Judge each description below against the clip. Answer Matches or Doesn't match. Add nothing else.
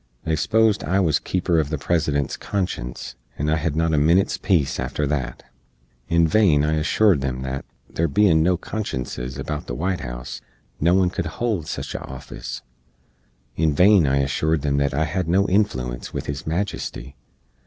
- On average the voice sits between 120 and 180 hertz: Doesn't match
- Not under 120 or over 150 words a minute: Doesn't match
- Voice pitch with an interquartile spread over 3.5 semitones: Matches